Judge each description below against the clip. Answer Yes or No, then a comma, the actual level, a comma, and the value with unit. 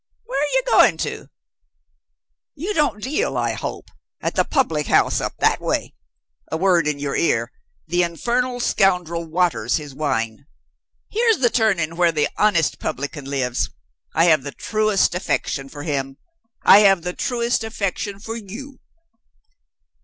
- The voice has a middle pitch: Yes, medium, 180 Hz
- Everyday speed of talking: Yes, average, 150 wpm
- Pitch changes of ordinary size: No, wide, 7.7 semitones